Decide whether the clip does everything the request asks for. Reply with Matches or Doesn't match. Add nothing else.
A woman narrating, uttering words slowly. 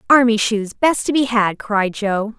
Doesn't match